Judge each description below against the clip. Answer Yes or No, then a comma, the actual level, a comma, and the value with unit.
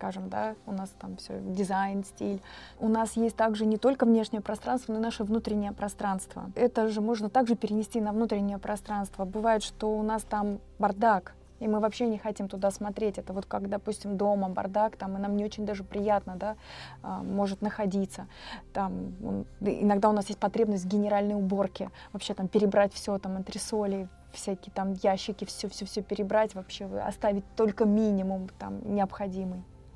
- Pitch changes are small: Yes, narrow, 1.7 semitones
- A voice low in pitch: No, high, 205 Hz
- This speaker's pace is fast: Yes, fast, 170 wpm